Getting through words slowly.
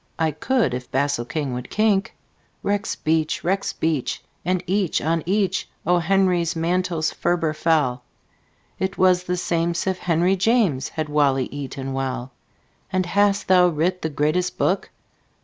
Yes: slow, 130 wpm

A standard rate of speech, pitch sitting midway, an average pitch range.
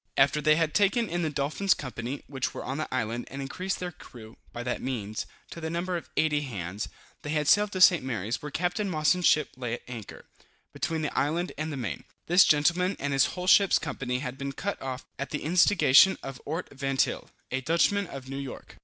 No: fast, 210 wpm; medium, 145 Hz; average, 4.9 semitones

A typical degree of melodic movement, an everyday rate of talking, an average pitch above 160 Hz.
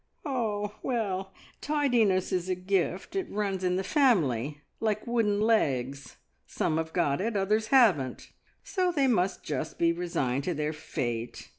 No: wide, 6.2 semitones; average, 155 wpm; high, 190 Hz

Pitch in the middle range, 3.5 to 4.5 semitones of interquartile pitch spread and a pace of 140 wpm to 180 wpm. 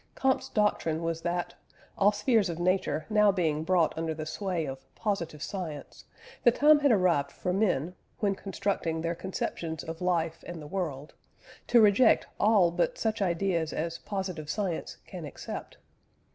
Yes: medium, 180 Hz; average, 3.9 semitones; average, 160 wpm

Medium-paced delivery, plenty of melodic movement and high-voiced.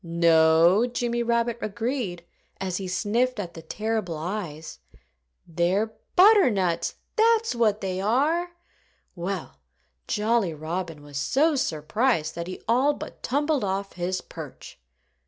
No: slow, 120 wpm; wide, 5.9 semitones; high, 200 Hz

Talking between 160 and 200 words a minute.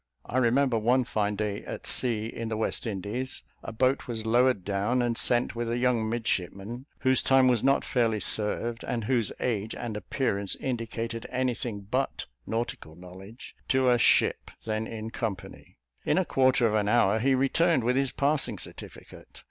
Yes: average, 170 wpm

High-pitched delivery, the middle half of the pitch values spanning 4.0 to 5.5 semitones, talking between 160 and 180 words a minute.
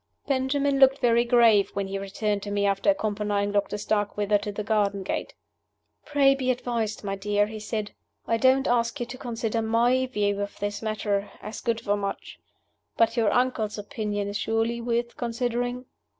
No: high, 220 Hz; average, 2.9 semitones; average, 175 wpm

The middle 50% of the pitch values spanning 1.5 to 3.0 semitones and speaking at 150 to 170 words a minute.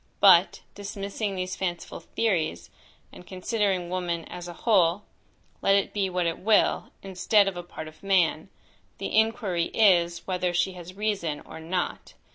Yes: narrow, 2.5 semitones; average, 155 wpm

